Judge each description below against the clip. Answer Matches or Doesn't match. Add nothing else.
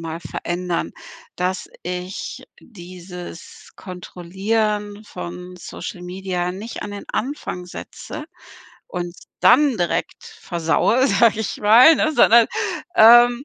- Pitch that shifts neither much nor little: Matches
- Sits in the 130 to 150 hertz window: Doesn't match